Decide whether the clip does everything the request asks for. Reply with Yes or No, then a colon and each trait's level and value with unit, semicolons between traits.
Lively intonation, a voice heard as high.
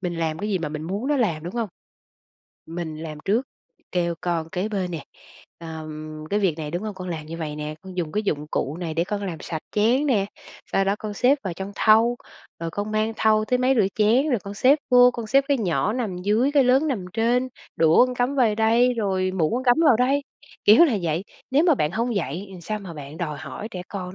Yes: wide, 6.1 semitones; high, 200 Hz